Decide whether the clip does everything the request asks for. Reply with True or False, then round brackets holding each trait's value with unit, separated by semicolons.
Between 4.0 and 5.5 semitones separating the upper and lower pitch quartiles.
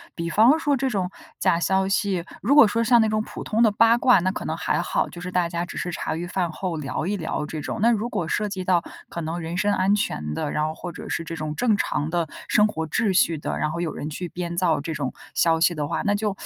True (4.3 semitones)